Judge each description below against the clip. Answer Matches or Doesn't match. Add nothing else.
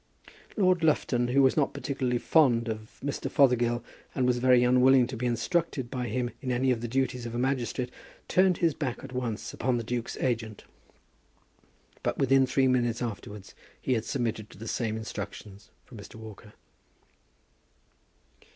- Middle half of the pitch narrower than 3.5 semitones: Matches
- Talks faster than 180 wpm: Doesn't match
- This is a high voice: Doesn't match